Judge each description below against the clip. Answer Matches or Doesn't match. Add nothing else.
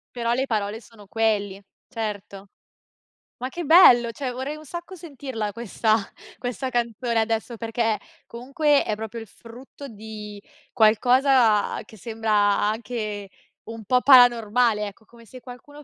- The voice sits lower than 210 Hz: Doesn't match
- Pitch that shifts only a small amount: Doesn't match